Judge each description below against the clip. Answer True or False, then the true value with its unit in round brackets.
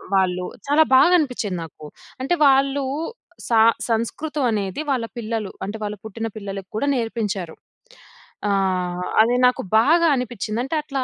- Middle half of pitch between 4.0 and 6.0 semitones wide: True (5.4 semitones)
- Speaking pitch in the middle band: False (225 Hz)